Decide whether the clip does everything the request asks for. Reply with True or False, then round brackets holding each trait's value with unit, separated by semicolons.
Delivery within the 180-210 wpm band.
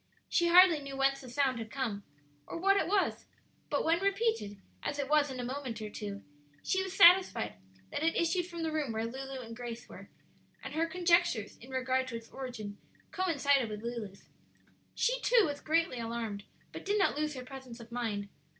True (195 wpm)